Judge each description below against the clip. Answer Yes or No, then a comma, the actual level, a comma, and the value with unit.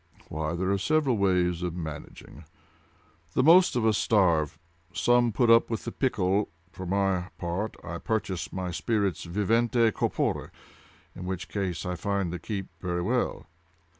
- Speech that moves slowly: No, average, 155 wpm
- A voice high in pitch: No, very low, 95 Hz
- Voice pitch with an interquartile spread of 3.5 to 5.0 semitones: Yes, average, 4.2 semitones